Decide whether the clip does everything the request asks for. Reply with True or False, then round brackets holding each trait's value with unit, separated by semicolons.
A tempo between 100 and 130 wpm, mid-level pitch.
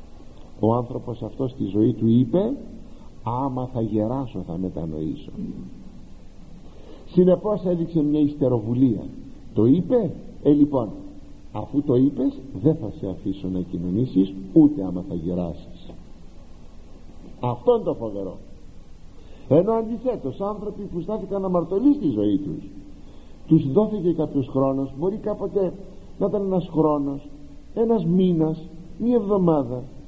True (120 wpm; 145 Hz)